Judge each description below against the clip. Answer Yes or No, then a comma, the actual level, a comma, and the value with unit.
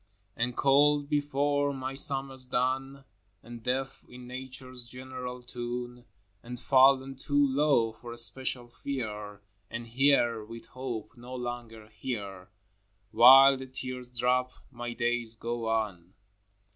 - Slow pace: Yes, slow, 130 wpm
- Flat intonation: Yes, narrow, 2.2 semitones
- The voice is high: No, low, 125 Hz